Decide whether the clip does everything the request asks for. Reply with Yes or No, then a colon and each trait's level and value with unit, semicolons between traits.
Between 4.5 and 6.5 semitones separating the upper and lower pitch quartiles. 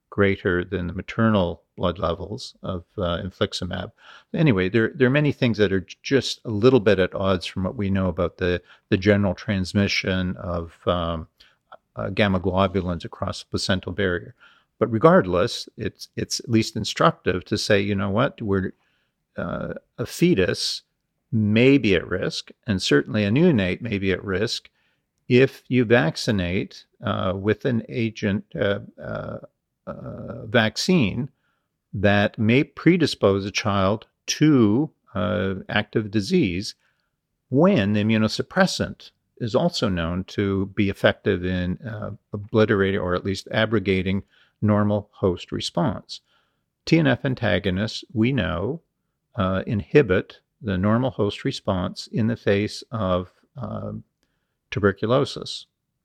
No: average, 3.3 semitones